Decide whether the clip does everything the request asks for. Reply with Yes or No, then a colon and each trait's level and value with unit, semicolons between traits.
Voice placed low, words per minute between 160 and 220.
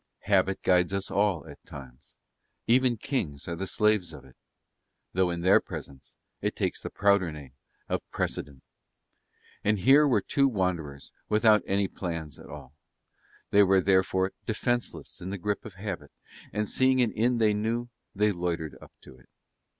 Yes: very low, 95 Hz; average, 165 wpm